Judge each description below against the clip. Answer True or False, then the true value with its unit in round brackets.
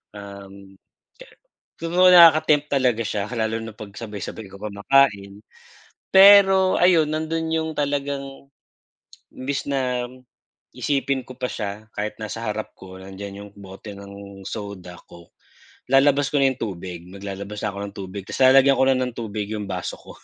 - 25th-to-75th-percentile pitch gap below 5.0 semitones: False (5.6 semitones)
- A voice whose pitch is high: False (110 Hz)